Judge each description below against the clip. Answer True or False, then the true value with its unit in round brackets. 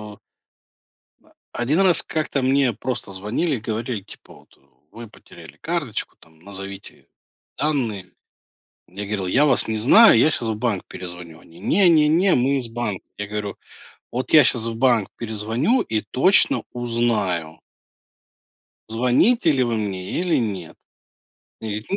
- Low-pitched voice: True (115 Hz)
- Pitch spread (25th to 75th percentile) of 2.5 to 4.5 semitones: False (5.0 semitones)